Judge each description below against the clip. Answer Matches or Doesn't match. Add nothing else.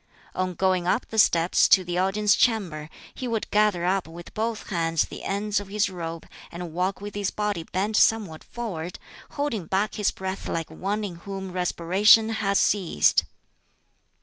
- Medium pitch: Doesn't match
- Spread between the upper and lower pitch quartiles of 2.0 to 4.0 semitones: Matches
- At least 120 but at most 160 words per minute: Doesn't match